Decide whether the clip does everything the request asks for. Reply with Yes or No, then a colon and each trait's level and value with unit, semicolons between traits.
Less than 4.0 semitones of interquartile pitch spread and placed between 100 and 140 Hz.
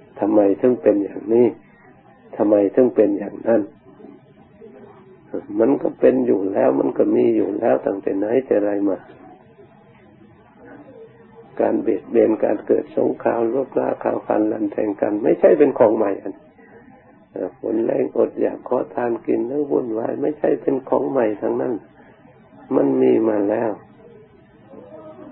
Yes: narrow, 2.4 semitones; low, 110 Hz